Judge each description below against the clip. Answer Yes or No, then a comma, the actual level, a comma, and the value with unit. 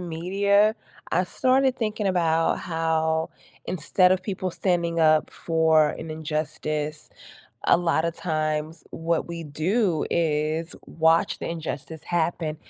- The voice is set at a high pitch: No, medium, 165 Hz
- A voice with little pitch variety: Yes, narrow, 2.3 semitones